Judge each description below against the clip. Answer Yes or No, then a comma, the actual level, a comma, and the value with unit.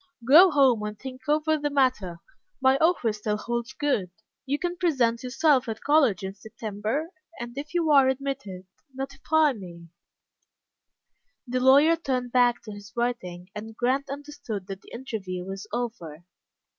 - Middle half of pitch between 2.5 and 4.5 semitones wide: No, average, 5.1 semitones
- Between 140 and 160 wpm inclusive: Yes, average, 150 wpm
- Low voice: No, high, 245 Hz